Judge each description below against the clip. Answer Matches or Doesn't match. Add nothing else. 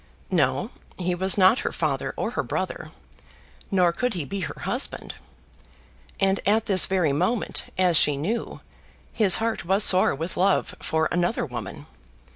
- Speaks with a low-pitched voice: Doesn't match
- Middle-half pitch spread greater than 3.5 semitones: Doesn't match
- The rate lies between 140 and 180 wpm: Matches